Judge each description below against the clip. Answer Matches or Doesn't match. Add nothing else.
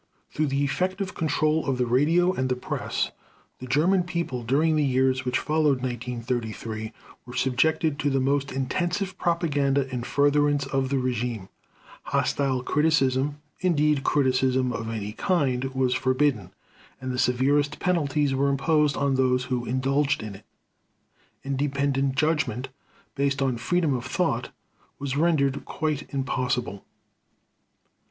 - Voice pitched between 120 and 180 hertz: Matches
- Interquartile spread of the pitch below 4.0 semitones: Matches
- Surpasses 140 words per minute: Doesn't match